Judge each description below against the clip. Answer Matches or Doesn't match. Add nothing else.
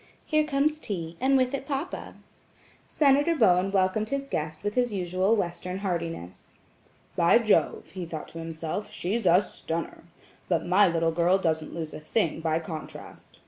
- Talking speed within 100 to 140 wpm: Doesn't match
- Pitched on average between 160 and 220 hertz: Matches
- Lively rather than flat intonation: Matches